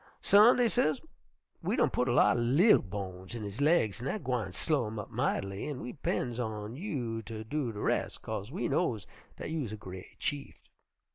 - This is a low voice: Yes, low, 120 Hz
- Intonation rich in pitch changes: Yes, wide, 5.8 semitones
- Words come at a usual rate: No, fast, 210 wpm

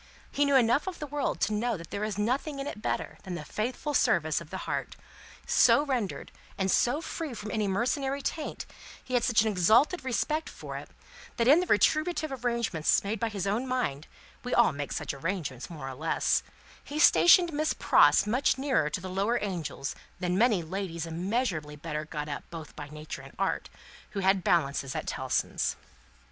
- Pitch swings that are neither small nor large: No, wide, 8.0 semitones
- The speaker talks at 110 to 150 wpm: No, average, 190 wpm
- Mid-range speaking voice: No, high, 210 Hz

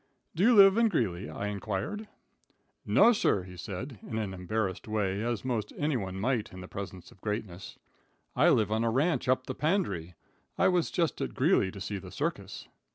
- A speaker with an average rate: Yes, average, 190 wpm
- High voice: No, low, 110 Hz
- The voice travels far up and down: Yes, wide, 6.5 semitones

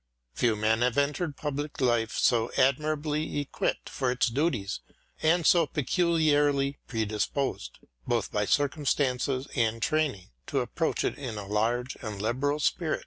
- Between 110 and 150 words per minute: Yes, average, 140 wpm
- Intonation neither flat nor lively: Yes, average, 4.5 semitones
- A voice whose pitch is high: No, low, 135 Hz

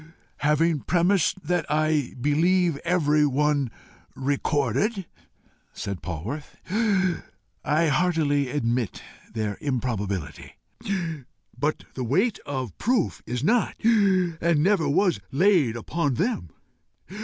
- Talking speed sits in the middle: No, slow, 95 wpm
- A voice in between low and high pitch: Yes, medium, 150 Hz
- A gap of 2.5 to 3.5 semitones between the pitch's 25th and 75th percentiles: No, average, 5.3 semitones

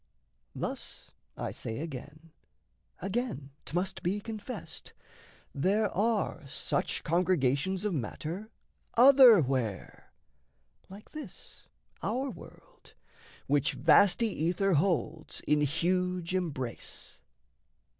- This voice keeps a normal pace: No, slow, 85 wpm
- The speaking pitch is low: No, medium, 180 Hz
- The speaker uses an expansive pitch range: Yes, wide, 5.7 semitones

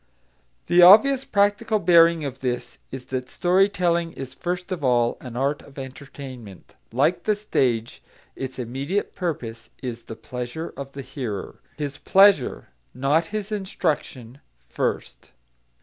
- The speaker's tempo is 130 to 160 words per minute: Yes, slow, 135 wpm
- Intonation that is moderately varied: No, wide, 6.0 semitones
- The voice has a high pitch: No, medium, 140 Hz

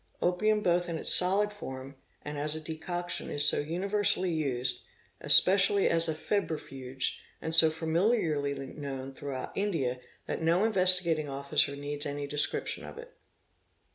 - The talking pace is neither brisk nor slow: Yes, average, 150 wpm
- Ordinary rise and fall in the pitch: Yes, average, 4.4 semitones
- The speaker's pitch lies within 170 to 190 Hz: No, medium, 160 Hz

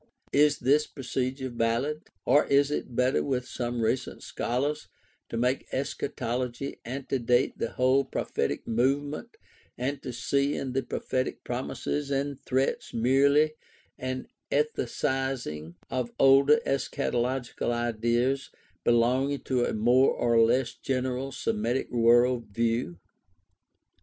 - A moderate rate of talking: No, slow, 115 wpm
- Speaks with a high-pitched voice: No, low, 130 Hz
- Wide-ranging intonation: No, narrow, 2.4 semitones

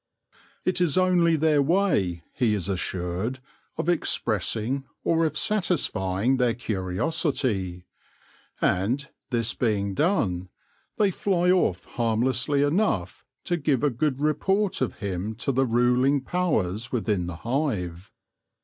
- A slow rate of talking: Yes, slow, 120 wpm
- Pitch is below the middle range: Yes, low, 125 Hz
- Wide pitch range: Yes, wide, 7.9 semitones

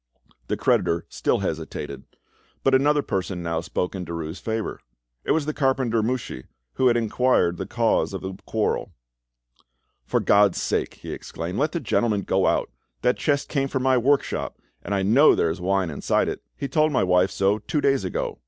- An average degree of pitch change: No, wide, 6.5 semitones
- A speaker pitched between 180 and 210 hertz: No, low, 110 Hz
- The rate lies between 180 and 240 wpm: Yes, average, 185 wpm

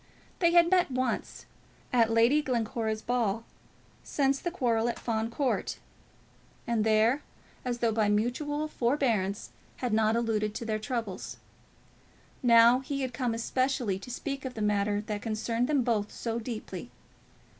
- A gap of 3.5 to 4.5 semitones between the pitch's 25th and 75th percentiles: No, average, 2.9 semitones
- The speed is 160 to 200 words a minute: No, average, 145 wpm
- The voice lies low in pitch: No, high, 235 Hz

